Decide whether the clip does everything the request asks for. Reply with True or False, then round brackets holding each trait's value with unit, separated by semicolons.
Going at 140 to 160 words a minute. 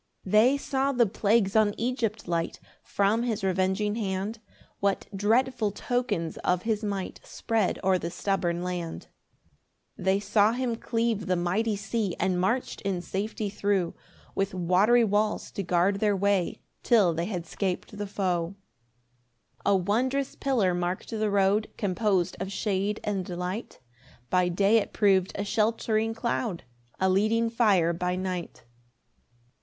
True (150 wpm)